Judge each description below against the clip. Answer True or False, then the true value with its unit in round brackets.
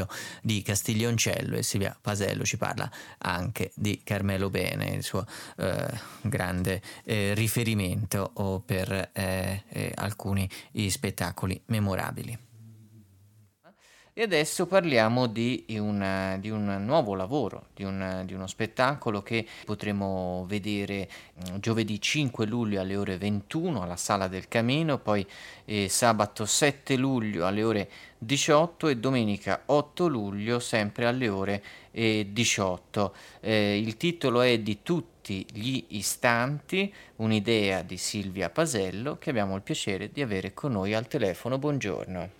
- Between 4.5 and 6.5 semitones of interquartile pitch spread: False (3.7 semitones)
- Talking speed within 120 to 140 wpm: True (125 wpm)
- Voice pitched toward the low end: True (105 Hz)